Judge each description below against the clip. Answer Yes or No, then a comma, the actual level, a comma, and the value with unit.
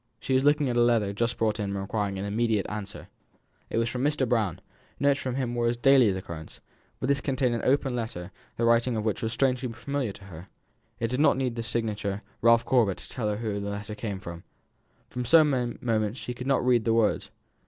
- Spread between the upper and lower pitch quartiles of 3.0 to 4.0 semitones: Yes, average, 3.4 semitones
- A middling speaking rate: No, fast, 225 wpm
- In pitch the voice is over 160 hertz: No, low, 115 Hz